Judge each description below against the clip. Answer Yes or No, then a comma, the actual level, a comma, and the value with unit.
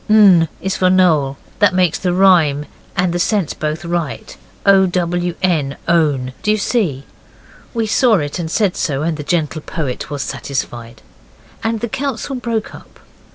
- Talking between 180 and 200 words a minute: No, average, 165 wpm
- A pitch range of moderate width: Yes, average, 4.9 semitones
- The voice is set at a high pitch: No, medium, 175 Hz